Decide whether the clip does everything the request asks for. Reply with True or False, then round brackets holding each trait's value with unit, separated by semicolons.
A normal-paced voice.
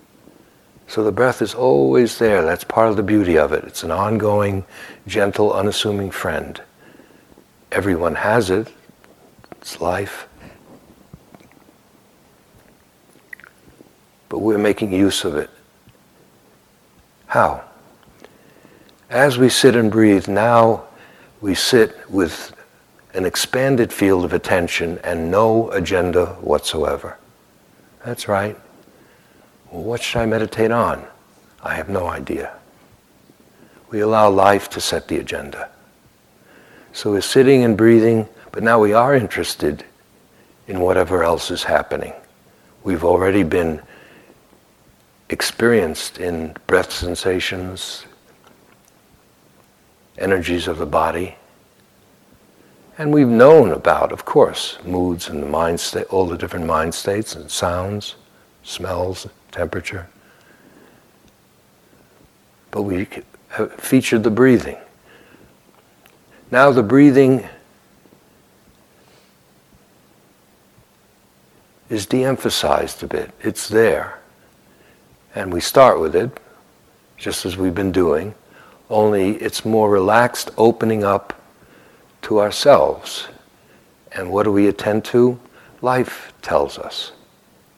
False (105 wpm)